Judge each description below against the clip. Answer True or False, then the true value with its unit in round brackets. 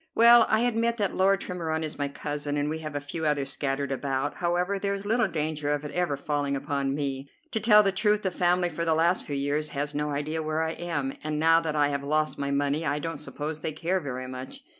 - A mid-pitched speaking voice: True (155 Hz)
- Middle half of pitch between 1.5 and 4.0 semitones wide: True (3.6 semitones)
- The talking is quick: True (240 wpm)